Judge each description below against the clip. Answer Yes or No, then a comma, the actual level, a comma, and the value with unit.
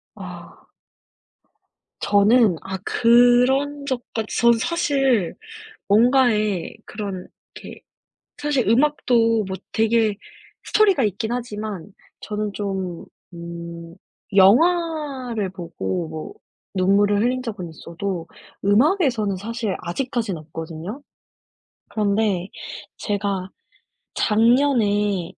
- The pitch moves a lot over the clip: No, average, 4.4 semitones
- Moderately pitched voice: No, high, 215 Hz